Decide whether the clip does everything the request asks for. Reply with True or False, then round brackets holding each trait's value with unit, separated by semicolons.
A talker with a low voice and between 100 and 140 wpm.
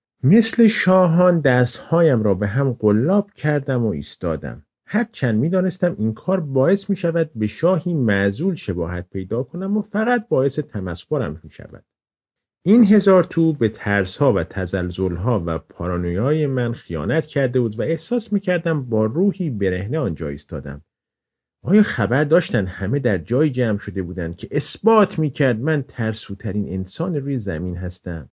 False (130 Hz; 150 wpm)